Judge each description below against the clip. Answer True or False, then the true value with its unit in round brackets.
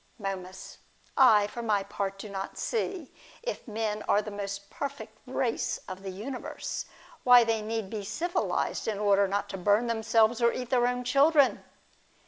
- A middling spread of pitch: True (3.7 semitones)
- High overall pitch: True (220 Hz)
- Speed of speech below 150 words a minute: False (165 wpm)